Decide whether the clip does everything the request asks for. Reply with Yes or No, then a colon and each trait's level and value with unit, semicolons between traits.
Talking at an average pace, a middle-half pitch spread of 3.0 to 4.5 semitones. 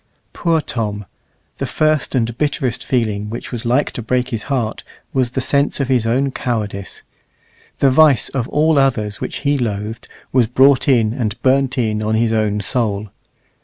Yes: average, 170 wpm; average, 3.8 semitones